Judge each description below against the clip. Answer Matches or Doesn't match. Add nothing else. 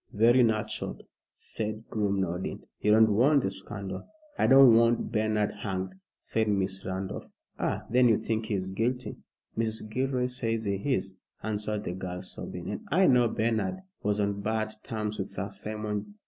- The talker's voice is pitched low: Matches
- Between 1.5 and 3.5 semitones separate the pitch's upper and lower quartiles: Matches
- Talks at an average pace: Matches